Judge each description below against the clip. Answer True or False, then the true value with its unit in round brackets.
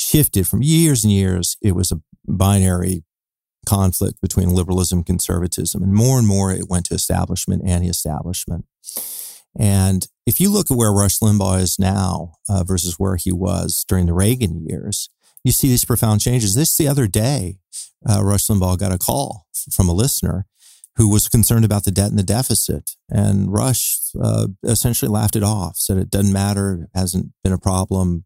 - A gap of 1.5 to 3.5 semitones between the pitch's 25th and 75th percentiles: True (3.1 semitones)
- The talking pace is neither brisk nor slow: True (180 wpm)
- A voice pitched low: True (100 Hz)